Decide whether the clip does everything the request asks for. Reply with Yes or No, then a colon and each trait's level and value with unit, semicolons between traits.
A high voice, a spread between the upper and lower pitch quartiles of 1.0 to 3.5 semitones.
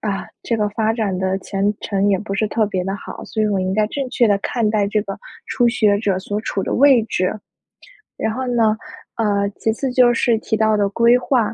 Yes: high, 215 Hz; narrow, 2.5 semitones